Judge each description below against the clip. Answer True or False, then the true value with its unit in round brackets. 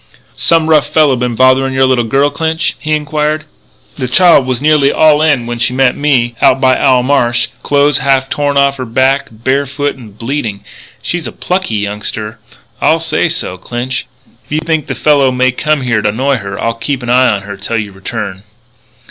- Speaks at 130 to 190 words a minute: False (200 wpm)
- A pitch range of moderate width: True (3.6 semitones)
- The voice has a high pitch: False (130 Hz)